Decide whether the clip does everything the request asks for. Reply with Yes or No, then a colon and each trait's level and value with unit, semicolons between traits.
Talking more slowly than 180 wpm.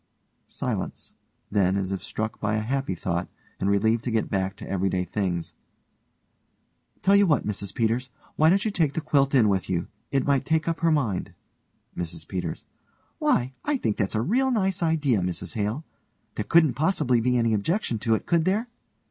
No: average, 185 wpm